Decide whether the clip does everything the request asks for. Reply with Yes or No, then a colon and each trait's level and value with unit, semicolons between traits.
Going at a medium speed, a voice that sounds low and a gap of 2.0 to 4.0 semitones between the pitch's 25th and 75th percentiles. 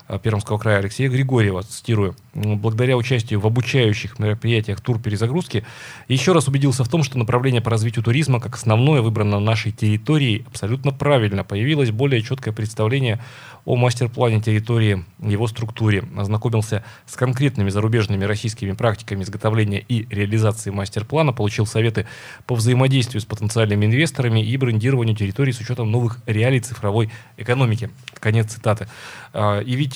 Yes: average, 135 wpm; low, 115 Hz; average, 3.0 semitones